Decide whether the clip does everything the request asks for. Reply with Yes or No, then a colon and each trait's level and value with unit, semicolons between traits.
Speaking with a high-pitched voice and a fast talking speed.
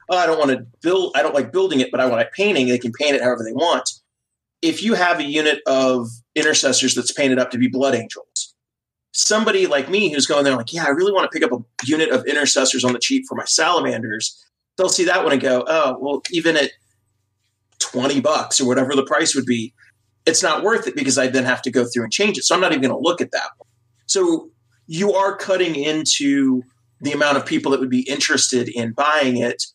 No: low, 135 Hz; fast, 240 wpm